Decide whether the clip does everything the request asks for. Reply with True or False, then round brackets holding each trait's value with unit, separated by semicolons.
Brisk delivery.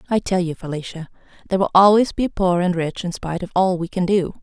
True (245 wpm)